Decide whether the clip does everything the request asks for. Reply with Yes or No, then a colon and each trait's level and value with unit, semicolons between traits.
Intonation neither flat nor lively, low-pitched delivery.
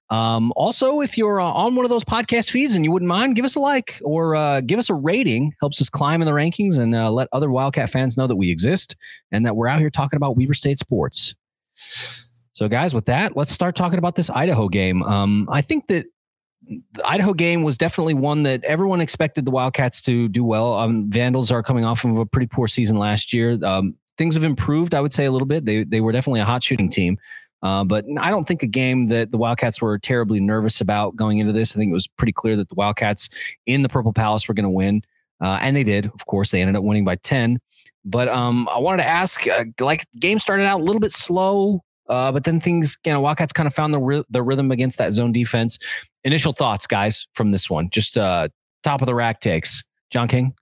No: wide, 6.0 semitones; low, 130 Hz